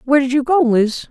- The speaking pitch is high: Yes, very high, 265 Hz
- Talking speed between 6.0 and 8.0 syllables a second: Yes, 6.1 syllables/s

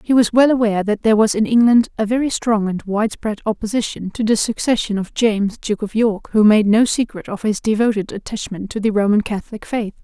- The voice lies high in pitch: Yes, high, 215 Hz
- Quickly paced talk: Yes, fast, 215 wpm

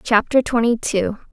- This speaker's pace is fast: No, slow, 135 wpm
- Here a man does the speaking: No, female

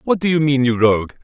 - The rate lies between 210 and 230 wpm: No, fast, 290 wpm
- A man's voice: Yes, male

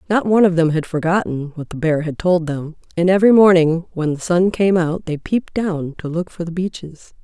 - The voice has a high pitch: No, medium, 170 Hz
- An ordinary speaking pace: No, fast, 230 wpm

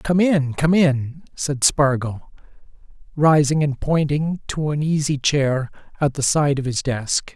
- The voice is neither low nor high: Yes, medium, 145 Hz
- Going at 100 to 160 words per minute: Yes, average, 155 wpm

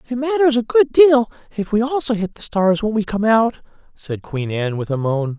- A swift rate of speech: Yes, fast, 235 wpm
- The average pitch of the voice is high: Yes, high, 195 Hz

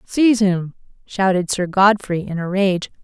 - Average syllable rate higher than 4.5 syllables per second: No, 4.3 syllables/s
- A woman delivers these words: Yes, female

